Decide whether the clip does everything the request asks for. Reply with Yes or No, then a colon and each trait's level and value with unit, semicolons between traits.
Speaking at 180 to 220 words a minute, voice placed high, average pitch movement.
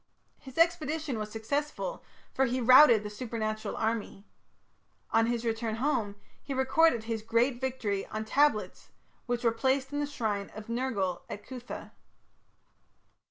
No: average, 140 wpm; high, 235 Hz; average, 3.5 semitones